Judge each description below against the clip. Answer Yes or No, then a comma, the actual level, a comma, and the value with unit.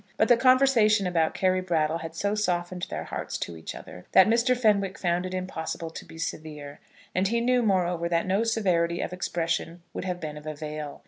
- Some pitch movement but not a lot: Yes, average, 4.0 semitones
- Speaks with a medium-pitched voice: Yes, medium, 180 Hz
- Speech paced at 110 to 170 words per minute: No, average, 200 wpm